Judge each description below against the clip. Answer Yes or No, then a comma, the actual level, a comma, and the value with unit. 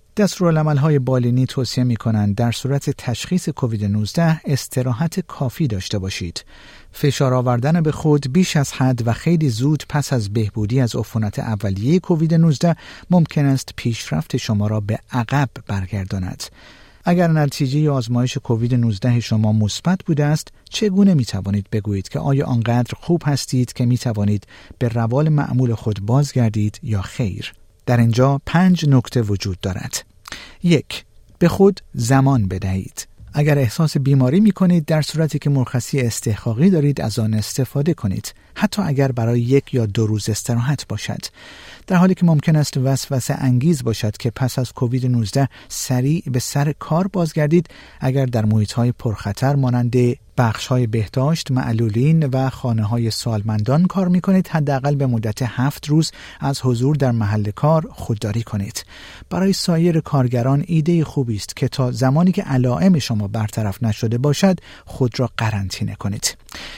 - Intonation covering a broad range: No, average, 4.9 semitones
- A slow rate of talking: No, fast, 155 wpm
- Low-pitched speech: Yes, low, 130 Hz